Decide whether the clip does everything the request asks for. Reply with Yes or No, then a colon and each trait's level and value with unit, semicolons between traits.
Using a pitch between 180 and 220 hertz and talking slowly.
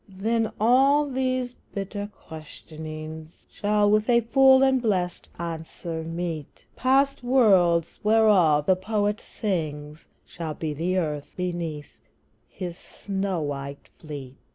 Yes: medium, 185 Hz; slow, 115 wpm